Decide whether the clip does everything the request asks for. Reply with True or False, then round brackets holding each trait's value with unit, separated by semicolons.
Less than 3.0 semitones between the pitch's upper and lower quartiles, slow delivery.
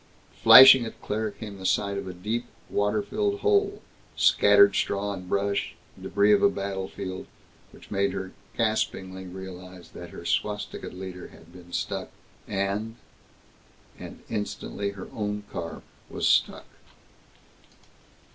True (2.5 semitones; 130 wpm)